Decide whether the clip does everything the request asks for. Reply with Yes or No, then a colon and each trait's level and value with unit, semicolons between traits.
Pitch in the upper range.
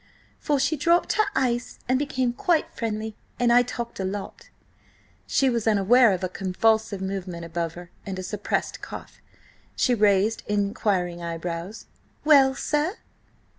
Yes: high, 215 Hz